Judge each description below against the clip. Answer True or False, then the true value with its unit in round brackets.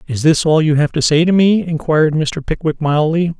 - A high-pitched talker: False (155 Hz)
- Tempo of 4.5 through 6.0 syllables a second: True (5.3 syllables/s)